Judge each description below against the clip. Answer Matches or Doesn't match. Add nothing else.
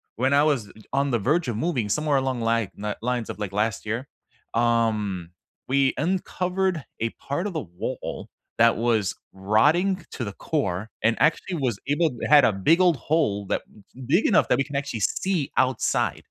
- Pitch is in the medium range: Doesn't match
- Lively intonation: Matches